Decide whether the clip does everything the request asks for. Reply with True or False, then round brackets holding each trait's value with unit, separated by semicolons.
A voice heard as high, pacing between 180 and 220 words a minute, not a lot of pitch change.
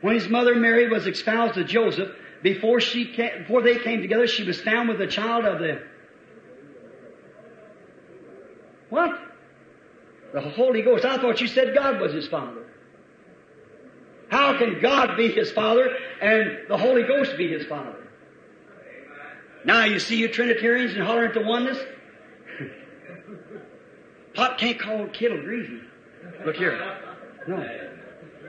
False (235 Hz; 135 wpm; 2.3 semitones)